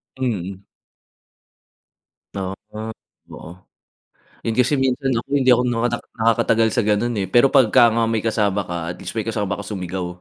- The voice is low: Yes, low, 115 Hz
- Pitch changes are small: No, average, 3.1 semitones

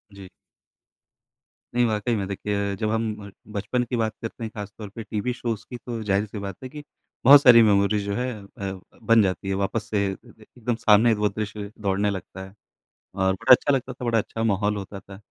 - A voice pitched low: Yes, low, 105 Hz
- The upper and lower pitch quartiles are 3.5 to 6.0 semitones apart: No, narrow, 2.5 semitones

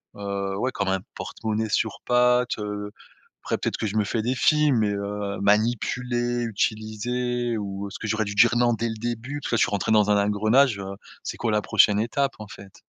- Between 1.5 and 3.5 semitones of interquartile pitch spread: Yes, average, 2.9 semitones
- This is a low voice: Yes, low, 110 Hz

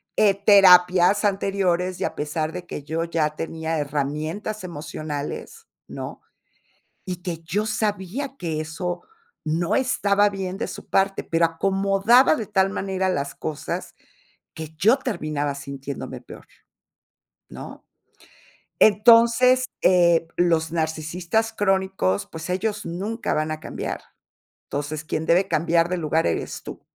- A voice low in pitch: No, medium, 180 Hz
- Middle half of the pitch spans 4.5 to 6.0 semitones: No, average, 4.1 semitones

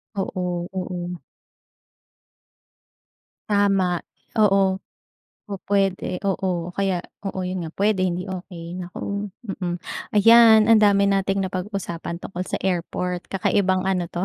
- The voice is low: No, high, 190 Hz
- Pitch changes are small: Yes, narrow, 1.8 semitones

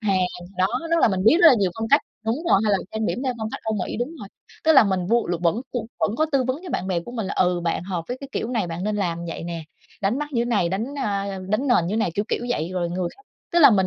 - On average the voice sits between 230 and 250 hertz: No, high, 210 Hz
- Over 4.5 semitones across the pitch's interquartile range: Yes, average, 4.9 semitones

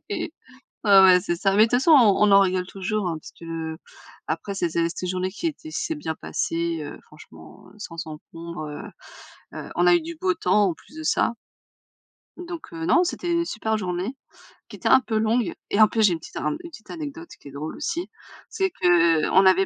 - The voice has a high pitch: Yes, high, 195 Hz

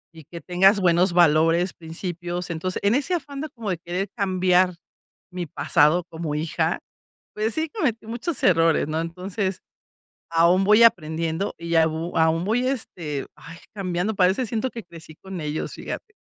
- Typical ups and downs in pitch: Yes, average, 3.8 semitones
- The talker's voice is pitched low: No, medium, 180 Hz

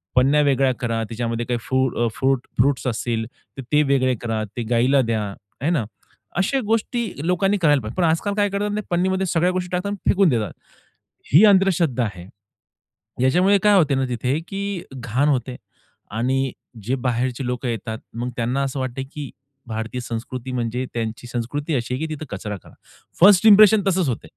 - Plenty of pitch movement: Yes, wide, 6.9 semitones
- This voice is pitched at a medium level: No, low, 130 Hz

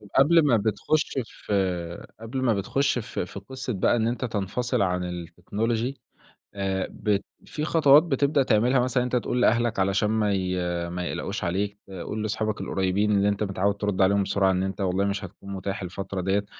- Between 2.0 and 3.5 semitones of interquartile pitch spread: No, average, 4.0 semitones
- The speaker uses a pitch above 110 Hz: No, low, 100 Hz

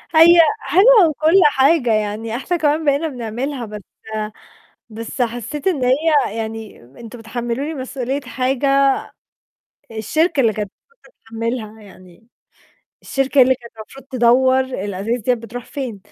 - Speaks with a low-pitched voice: No, very high, 250 Hz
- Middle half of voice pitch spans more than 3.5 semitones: Yes, average, 4.1 semitones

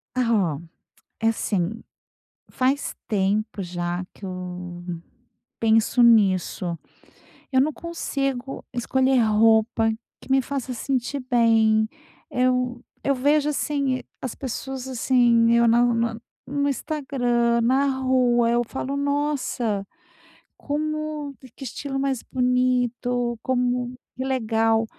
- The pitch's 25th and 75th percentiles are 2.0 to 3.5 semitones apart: Yes, average, 3.0 semitones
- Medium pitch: No, high, 245 Hz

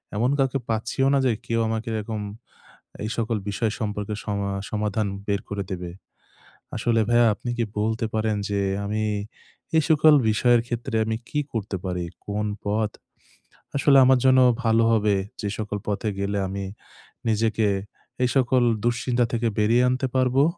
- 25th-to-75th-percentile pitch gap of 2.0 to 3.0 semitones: Yes, narrow, 2.6 semitones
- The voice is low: Yes, low, 110 Hz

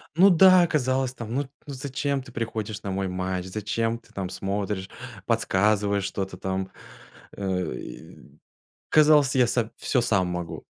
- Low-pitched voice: Yes, low, 110 Hz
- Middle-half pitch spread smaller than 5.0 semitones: No, wide, 5.6 semitones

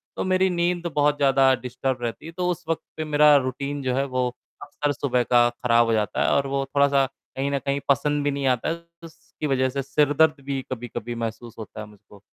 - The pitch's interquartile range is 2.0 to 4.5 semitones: Yes, average, 2.8 semitones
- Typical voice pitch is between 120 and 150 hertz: Yes, medium, 140 Hz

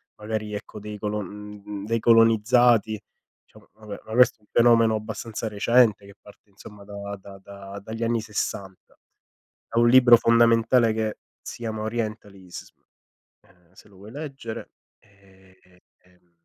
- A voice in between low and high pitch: No, low, 105 Hz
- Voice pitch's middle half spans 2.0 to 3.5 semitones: Yes, narrow, 2.4 semitones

